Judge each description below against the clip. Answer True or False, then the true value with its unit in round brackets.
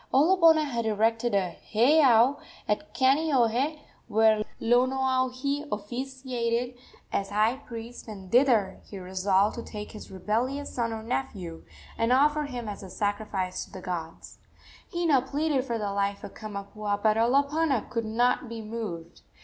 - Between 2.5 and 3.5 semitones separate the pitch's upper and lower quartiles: False (4.2 semitones)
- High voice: True (230 Hz)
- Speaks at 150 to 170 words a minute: False (140 wpm)